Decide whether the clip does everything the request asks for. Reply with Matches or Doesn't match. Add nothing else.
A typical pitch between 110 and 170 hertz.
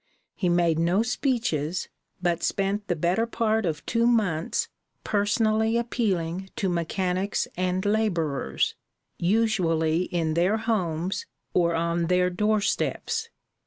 Doesn't match